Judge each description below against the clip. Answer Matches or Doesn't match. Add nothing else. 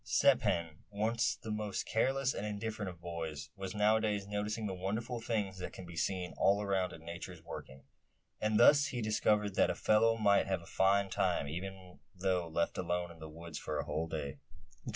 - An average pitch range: Matches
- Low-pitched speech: Matches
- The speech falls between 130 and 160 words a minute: Doesn't match